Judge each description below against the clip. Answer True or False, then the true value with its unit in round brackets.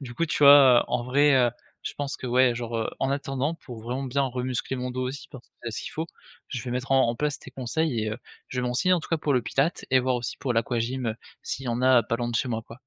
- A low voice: True (125 Hz)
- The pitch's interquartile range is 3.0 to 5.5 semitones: False (2.4 semitones)